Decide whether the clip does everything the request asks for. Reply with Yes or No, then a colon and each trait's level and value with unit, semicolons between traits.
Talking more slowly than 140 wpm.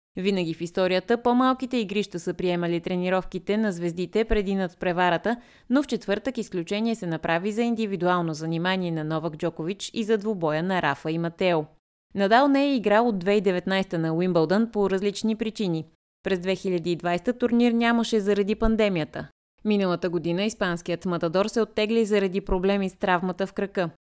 No: average, 150 wpm